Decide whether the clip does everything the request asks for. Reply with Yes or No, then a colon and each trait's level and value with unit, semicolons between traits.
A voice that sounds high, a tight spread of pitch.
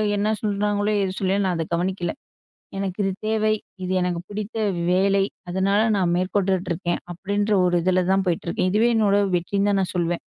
Yes: high, 195 Hz; narrow, 2.2 semitones